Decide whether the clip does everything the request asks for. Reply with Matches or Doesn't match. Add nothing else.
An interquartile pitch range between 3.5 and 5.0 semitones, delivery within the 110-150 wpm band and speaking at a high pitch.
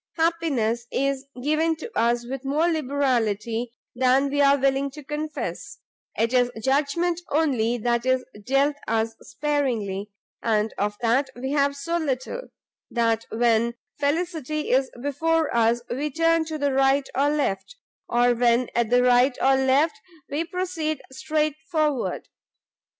Matches